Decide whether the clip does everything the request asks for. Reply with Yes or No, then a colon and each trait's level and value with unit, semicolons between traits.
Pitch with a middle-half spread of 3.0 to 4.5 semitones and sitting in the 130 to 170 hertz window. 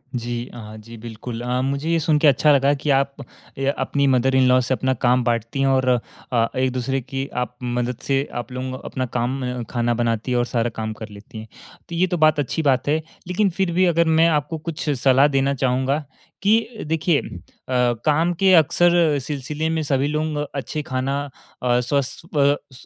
Yes: average, 3.6 semitones; low, 135 Hz